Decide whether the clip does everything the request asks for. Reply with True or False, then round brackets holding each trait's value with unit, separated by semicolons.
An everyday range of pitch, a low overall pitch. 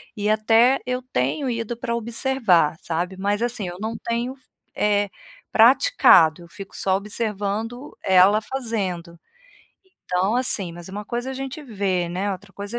False (4.1 semitones; 210 Hz)